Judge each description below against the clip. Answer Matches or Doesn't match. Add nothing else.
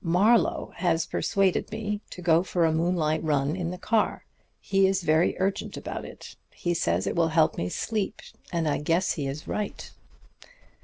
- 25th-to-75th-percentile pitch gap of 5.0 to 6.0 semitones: Doesn't match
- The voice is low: Doesn't match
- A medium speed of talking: Matches